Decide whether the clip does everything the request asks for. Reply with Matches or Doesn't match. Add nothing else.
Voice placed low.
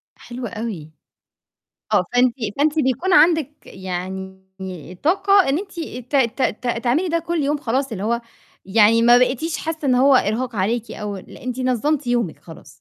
Doesn't match